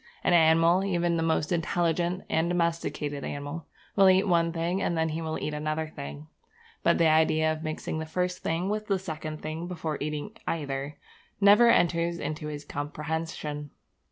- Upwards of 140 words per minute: Yes, average, 170 wpm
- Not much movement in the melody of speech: Yes, narrow, 2.2 semitones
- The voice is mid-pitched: Yes, medium, 160 Hz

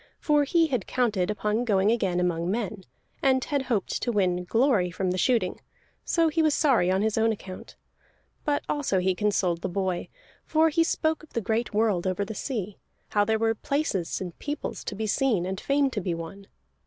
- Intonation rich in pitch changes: Yes, wide, 6.0 semitones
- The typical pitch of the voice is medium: No, high, 215 Hz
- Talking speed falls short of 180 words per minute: No, average, 200 wpm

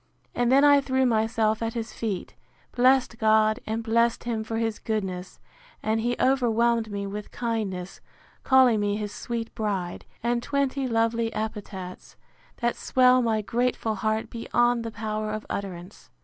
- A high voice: Yes, high, 225 Hz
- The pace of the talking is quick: No, average, 150 wpm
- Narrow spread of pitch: Yes, narrow, 2.0 semitones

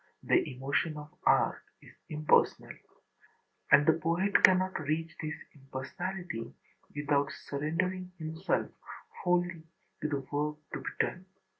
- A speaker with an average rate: No, slow, 120 wpm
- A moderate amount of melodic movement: Yes, average, 3.5 semitones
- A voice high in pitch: No, medium, 155 Hz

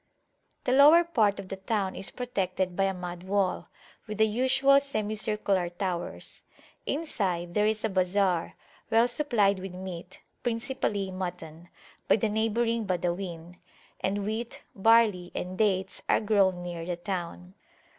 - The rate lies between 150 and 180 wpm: No, average, 140 wpm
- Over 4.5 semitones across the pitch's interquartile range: No, average, 3.5 semitones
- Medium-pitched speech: No, high, 195 Hz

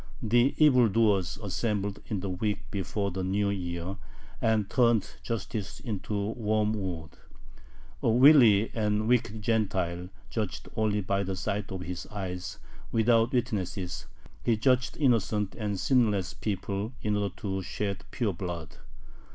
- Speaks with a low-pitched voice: Yes, low, 105 Hz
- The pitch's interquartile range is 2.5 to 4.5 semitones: Yes, average, 2.8 semitones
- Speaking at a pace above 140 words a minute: No, slow, 135 wpm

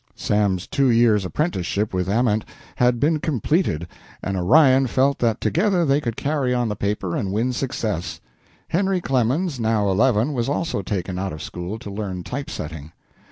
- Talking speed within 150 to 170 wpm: Yes, average, 165 wpm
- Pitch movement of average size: No, wide, 6.0 semitones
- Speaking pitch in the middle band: No, low, 115 Hz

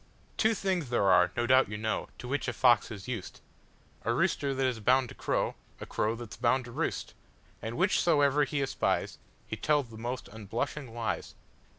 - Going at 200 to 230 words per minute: No, average, 170 wpm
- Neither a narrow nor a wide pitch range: Yes, average, 4.0 semitones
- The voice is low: Yes, low, 125 Hz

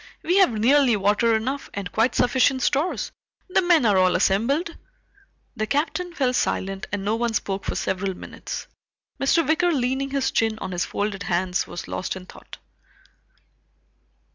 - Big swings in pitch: Yes, wide, 6.1 semitones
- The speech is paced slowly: No, average, 160 wpm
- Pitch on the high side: Yes, high, 230 Hz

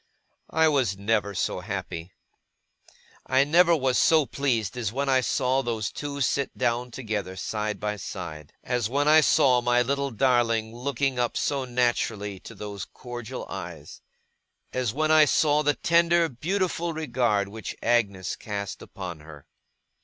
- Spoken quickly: No, average, 150 wpm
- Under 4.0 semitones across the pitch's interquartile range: No, average, 5.0 semitones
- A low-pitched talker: Yes, low, 125 Hz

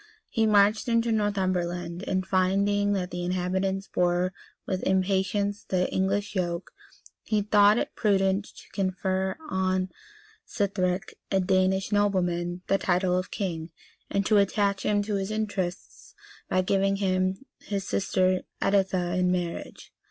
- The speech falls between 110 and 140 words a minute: Yes, slow, 135 wpm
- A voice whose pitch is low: No, high, 190 Hz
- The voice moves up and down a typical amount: No, narrow, 1.7 semitones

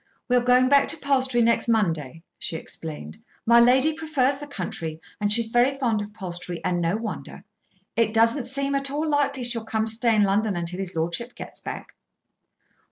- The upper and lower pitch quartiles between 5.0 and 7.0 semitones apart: Yes, wide, 5.4 semitones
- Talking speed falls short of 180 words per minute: No, average, 195 wpm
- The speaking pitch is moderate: No, high, 230 Hz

